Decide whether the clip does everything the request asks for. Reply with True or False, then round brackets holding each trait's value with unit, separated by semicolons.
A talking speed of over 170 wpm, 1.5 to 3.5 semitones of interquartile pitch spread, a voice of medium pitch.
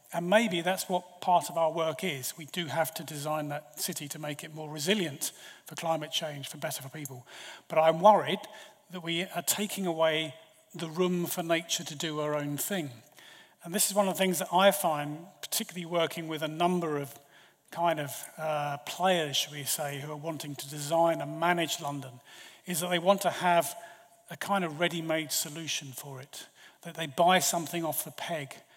True (200 wpm; 2.9 semitones; 165 Hz)